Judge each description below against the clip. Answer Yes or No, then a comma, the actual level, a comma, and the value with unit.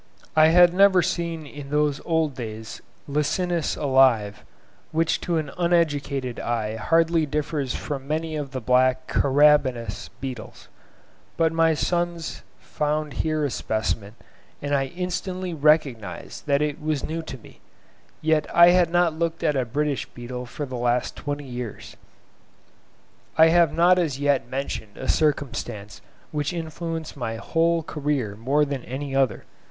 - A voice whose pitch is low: No, medium, 150 Hz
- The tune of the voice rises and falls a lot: No, average, 4.0 semitones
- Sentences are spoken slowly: No, average, 145 wpm